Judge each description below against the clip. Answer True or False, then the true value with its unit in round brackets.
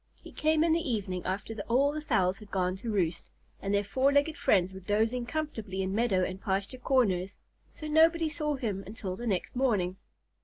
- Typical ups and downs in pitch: False (6.6 semitones)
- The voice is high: True (220 Hz)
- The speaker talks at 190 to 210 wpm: True (195 wpm)